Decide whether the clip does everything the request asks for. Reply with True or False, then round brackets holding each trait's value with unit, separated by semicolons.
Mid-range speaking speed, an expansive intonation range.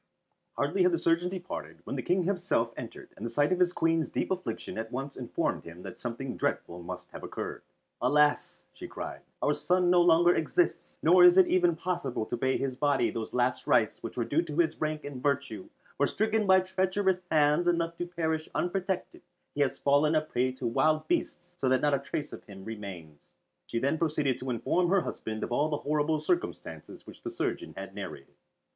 False (210 wpm; 5.7 semitones)